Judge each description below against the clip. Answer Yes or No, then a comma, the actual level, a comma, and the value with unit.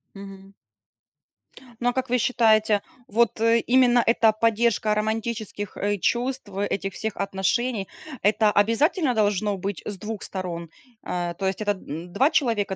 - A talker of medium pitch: No, high, 215 Hz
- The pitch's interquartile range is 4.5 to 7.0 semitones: No, average, 3.1 semitones